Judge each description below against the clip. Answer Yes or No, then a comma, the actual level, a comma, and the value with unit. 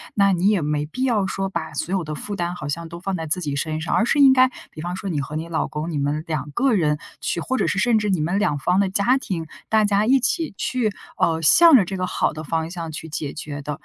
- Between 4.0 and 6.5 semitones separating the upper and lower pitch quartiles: Yes, average, 4.9 semitones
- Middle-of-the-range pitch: Yes, medium, 175 Hz